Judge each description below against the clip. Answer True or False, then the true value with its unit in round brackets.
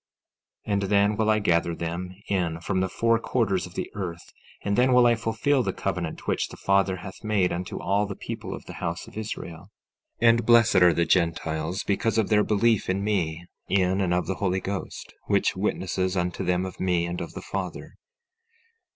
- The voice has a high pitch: False (95 Hz)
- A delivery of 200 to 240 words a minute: True (205 wpm)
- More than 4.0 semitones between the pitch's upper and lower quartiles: False (3.2 semitones)